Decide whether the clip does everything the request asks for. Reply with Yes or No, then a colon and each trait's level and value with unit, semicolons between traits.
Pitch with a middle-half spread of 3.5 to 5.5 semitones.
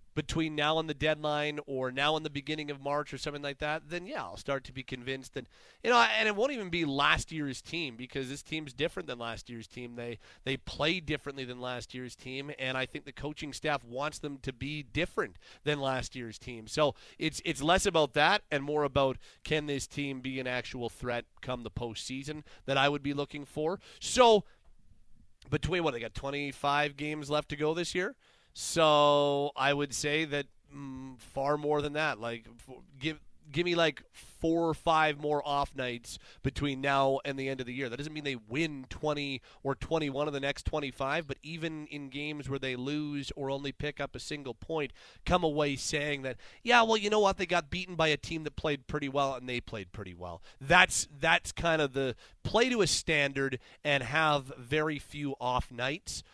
No: narrow, 2.6 semitones